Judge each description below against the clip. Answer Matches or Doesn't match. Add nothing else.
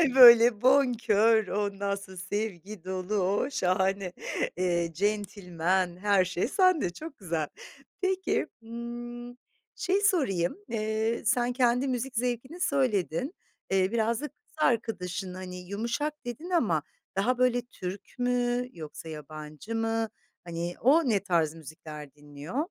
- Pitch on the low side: Doesn't match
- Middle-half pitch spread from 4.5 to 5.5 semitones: Matches